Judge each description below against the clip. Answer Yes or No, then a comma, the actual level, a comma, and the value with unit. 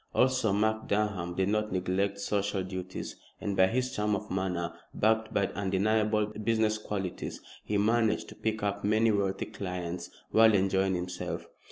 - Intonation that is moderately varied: No, narrow, 2.3 semitones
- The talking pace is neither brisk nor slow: Yes, average, 155 wpm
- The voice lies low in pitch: Yes, low, 100 Hz